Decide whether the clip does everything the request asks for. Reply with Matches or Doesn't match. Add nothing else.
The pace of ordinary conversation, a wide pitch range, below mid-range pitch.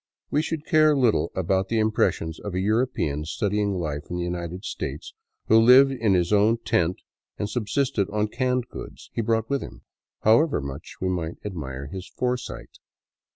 Matches